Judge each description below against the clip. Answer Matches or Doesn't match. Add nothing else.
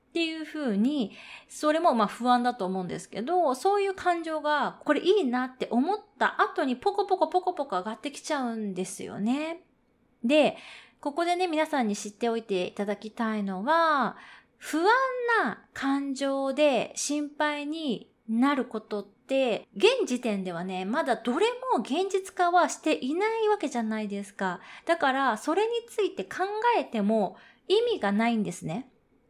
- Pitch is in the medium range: Doesn't match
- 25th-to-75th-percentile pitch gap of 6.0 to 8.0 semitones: Matches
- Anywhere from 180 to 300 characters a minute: Doesn't match